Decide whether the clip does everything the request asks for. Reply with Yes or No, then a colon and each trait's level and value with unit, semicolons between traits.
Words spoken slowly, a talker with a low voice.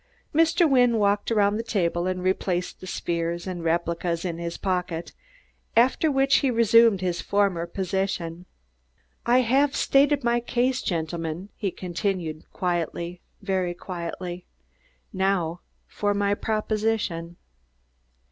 No: slow, 120 wpm; high, 190 Hz